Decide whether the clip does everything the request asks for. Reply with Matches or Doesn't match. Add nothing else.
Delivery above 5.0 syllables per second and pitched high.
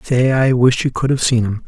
Doesn't match